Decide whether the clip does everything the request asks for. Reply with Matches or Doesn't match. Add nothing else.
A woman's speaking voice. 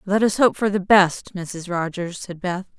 Matches